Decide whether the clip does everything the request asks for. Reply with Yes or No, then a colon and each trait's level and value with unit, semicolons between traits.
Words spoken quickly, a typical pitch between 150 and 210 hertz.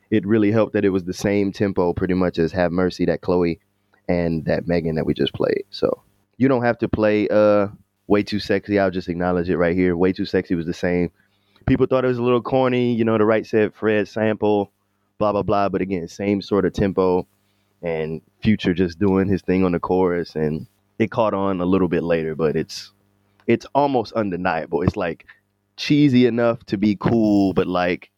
No: fast, 210 wpm; low, 100 Hz